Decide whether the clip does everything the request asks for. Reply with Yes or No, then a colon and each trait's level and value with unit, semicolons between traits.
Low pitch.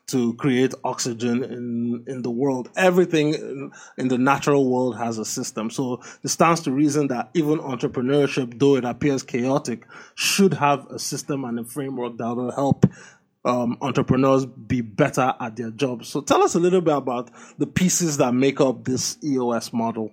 Yes: low, 130 Hz